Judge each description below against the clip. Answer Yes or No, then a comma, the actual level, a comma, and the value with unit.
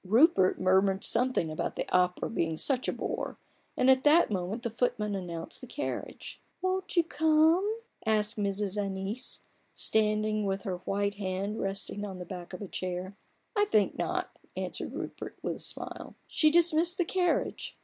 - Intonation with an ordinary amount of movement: No, wide, 7.3 semitones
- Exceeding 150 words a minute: Yes, average, 175 wpm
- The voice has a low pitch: No, high, 210 Hz